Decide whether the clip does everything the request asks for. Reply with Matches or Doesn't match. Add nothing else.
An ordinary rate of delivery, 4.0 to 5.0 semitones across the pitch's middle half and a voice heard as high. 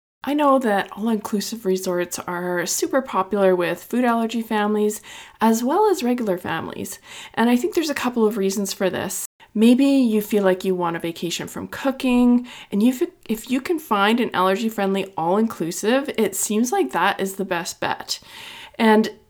Matches